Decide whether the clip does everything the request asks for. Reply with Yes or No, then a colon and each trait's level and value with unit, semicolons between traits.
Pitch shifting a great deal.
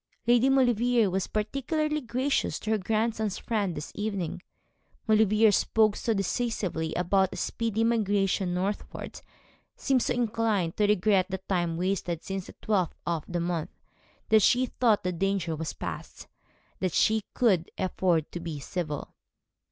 No: average, 4.1 semitones